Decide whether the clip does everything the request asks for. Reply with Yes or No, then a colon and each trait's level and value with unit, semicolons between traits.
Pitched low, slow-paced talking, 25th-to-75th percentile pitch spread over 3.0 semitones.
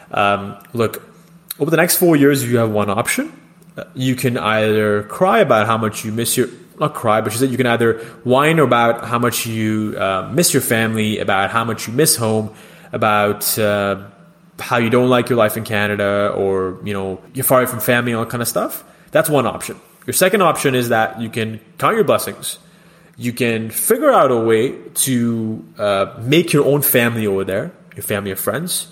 No: low, 115 Hz; average, 200 wpm; average, 4.2 semitones